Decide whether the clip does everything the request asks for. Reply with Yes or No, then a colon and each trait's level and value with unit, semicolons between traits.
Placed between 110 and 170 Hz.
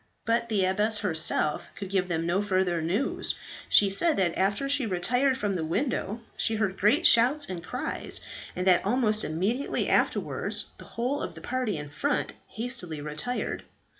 No: high, 205 Hz